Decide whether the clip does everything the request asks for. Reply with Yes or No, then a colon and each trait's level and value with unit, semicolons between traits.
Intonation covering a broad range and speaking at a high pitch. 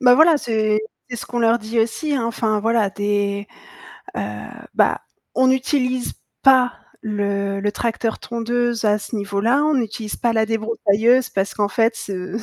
No: average, 2.8 semitones; high, 225 Hz